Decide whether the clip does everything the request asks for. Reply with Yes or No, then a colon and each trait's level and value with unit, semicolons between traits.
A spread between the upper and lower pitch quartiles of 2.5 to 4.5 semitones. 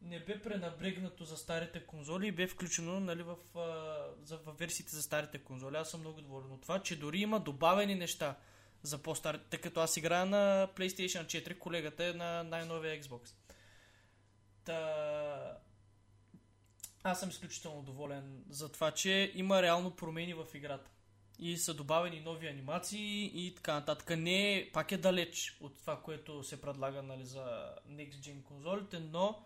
Yes: average, 3.5 semitones